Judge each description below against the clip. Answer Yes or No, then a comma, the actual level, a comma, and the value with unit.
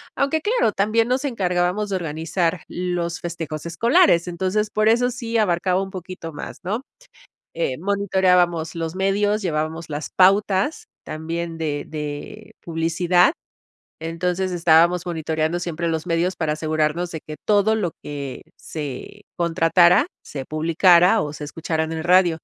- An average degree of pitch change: Yes, average, 3.2 semitones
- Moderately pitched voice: Yes, medium, 175 Hz